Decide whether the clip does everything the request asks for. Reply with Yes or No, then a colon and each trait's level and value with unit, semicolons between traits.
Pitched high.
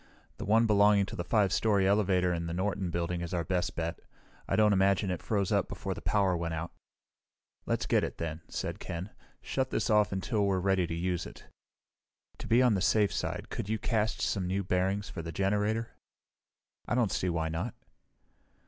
No: very low, 95 Hz